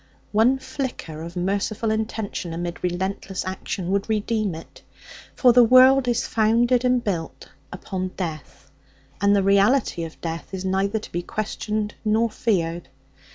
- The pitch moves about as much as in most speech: Yes, average, 4.3 semitones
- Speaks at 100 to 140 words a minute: No, average, 150 wpm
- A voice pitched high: Yes, high, 200 Hz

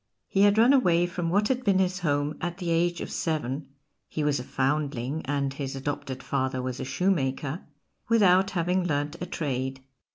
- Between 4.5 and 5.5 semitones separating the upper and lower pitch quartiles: Yes, average, 4.9 semitones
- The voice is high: No, medium, 155 Hz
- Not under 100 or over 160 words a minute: No, average, 190 wpm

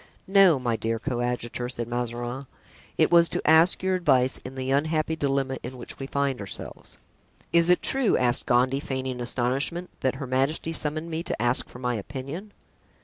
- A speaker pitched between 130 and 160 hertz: Yes, low, 135 Hz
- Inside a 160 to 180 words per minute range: Yes, average, 175 wpm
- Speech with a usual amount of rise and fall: Yes, average, 4.5 semitones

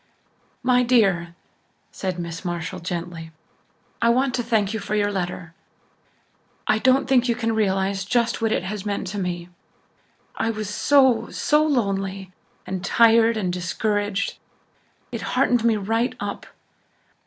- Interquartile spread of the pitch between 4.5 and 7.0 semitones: No, average, 3.9 semitones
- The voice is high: Yes, high, 205 Hz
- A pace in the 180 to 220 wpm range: No, average, 145 wpm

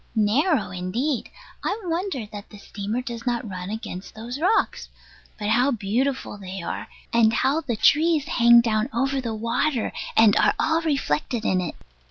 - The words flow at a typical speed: Yes, average, 165 wpm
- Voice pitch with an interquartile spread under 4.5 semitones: No, average, 4.8 semitones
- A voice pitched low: No, high, 235 Hz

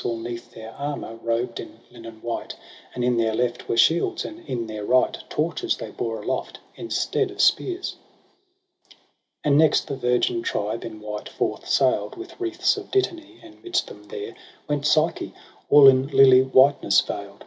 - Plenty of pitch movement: Yes, wide, 6.7 semitones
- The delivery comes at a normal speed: Yes, average, 175 wpm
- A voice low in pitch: Yes, low, 130 Hz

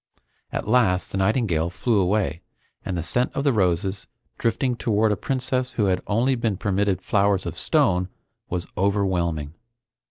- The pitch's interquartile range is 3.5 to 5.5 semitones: Yes, average, 4.1 semitones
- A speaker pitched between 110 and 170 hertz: No, low, 100 Hz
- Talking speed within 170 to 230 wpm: No, average, 155 wpm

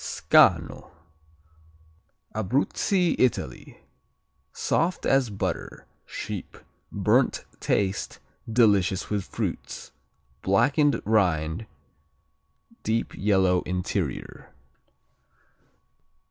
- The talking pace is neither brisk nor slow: No, slow, 65 wpm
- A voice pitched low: Yes, low, 105 Hz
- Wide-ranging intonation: No, average, 4.8 semitones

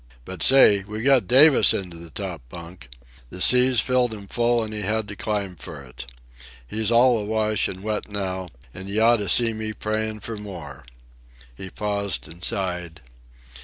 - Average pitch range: Yes, average, 3.3 semitones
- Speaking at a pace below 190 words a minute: Yes, average, 170 wpm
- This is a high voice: No, low, 105 Hz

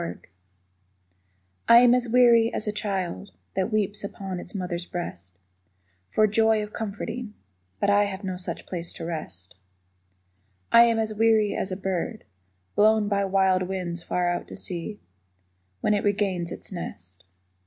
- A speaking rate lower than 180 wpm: Yes, average, 160 wpm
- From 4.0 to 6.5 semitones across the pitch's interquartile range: No, average, 3.4 semitones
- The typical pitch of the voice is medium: No, high, 200 Hz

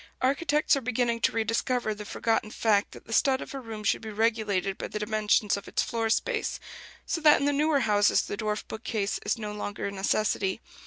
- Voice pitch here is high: Yes, high, 220 Hz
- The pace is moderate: No, fast, 210 wpm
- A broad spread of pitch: No, average, 3.2 semitones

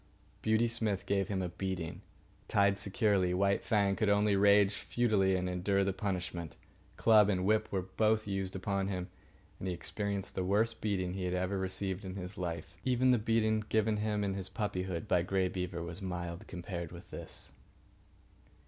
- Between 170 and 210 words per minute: Yes, average, 180 wpm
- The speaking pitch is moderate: No, very low, 95 Hz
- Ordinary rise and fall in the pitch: No, narrow, 2.3 semitones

